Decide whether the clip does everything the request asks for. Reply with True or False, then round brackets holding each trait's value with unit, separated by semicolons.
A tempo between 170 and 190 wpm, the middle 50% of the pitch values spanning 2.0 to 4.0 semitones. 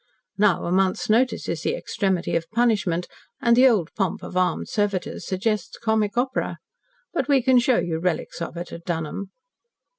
False (175 wpm; 5.0 semitones)